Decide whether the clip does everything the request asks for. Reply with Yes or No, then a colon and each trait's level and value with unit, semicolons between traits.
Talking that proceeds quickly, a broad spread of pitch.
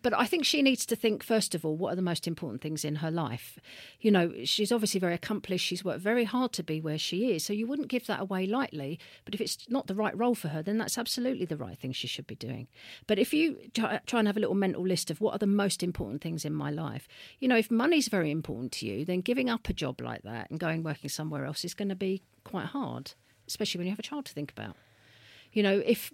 Yes: fast, 270 wpm; wide, 6.5 semitones